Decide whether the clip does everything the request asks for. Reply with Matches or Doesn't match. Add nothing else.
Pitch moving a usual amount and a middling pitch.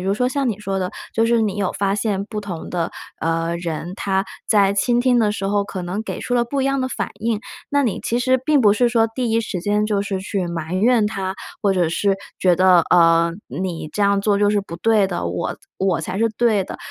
Doesn't match